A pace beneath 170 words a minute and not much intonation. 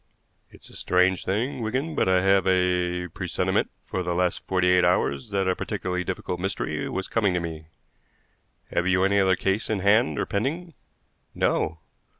No: average, 175 wpm; narrow, 2.0 semitones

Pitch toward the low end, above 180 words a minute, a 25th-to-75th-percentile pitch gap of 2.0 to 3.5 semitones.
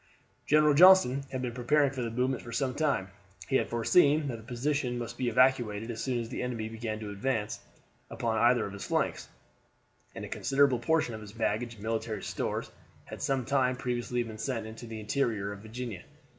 Yes: low, 120 Hz; average, 200 wpm; average, 3.1 semitones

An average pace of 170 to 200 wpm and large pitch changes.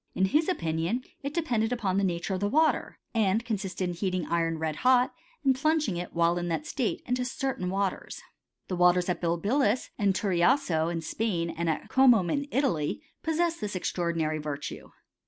Yes: average, 180 wpm; wide, 6.7 semitones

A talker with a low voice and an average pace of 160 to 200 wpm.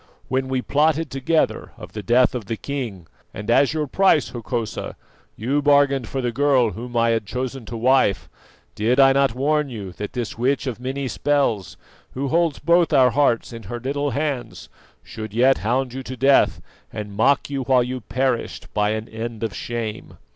Yes: low, 125 Hz; average, 185 wpm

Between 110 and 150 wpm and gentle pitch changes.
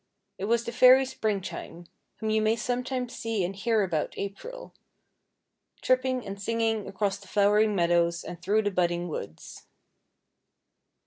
No: average, 140 wpm; average, 3.9 semitones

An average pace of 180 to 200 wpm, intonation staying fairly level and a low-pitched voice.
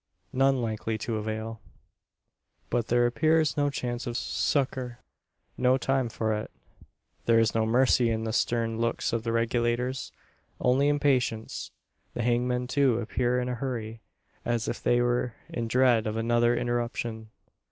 No: average, 150 wpm; narrow, 1.9 semitones; low, 120 Hz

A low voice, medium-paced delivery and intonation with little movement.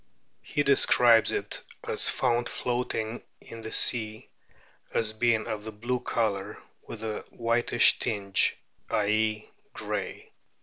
No: low, 110 Hz; slow, 125 wpm; narrow, 1.9 semitones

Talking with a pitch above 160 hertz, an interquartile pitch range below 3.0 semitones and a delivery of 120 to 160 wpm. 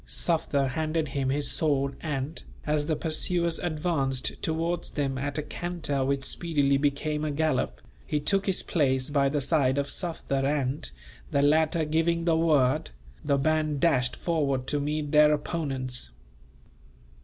No: medium, 150 Hz; narrow, 2.6 semitones; average, 150 wpm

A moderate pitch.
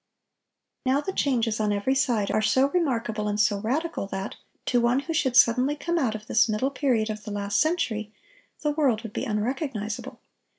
No: high, 235 Hz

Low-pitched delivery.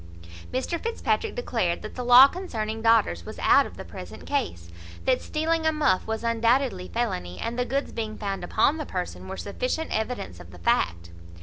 No: high, 230 Hz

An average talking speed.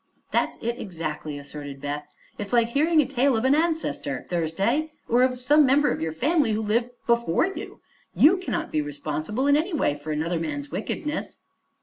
Yes: average, 185 wpm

